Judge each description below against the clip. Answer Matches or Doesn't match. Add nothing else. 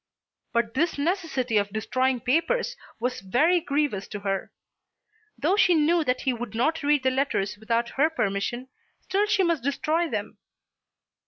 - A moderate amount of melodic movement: Doesn't match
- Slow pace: Doesn't match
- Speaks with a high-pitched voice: Matches